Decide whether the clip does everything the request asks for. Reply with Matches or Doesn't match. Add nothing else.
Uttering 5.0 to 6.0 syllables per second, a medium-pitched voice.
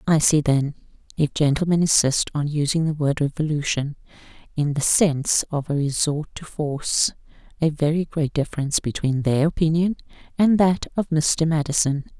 Matches